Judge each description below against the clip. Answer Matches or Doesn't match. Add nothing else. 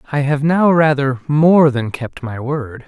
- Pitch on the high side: Doesn't match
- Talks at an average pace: Matches